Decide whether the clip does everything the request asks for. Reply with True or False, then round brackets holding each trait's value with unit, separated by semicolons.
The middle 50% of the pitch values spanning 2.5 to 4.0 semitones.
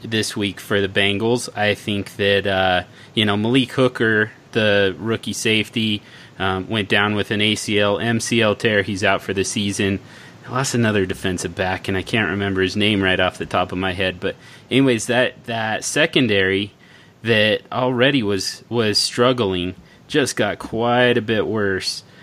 True (3.0 semitones)